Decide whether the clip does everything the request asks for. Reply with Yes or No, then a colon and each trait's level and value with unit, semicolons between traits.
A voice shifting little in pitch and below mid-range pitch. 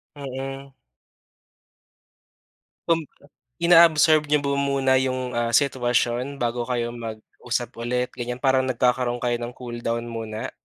Yes: narrow, 2.3 semitones; low, 125 Hz